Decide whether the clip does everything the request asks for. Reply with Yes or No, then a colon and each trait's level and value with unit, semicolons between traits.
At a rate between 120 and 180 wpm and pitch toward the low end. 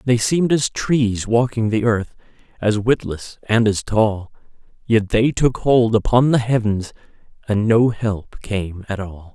Yes: average, 160 wpm; low, 110 Hz